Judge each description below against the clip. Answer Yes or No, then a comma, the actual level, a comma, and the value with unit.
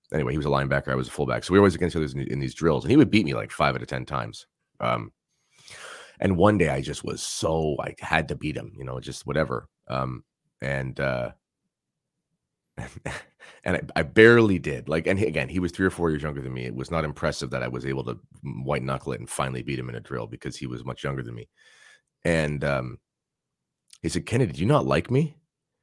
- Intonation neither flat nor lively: Yes, average, 3.8 semitones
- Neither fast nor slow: No, fast, 240 wpm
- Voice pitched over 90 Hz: No, very low, 70 Hz